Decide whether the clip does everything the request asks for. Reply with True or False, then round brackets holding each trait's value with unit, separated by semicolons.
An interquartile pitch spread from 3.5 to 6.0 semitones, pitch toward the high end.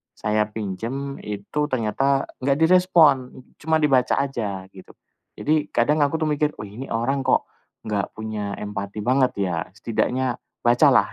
False (5.0 semitones; 125 Hz)